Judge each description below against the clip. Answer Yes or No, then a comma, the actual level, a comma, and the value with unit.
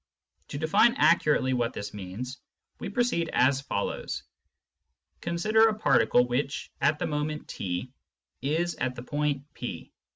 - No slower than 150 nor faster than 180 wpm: No, slow, 135 wpm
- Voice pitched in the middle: Yes, medium, 150 Hz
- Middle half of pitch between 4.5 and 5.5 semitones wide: Yes, average, 5.1 semitones